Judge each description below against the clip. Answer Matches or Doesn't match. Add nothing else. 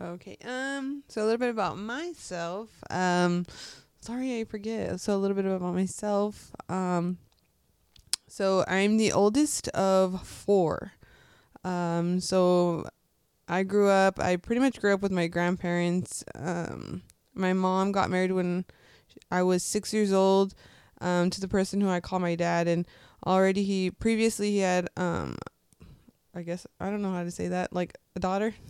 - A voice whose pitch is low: Doesn't match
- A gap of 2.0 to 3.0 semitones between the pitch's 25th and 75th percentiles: Matches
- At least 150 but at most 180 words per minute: Matches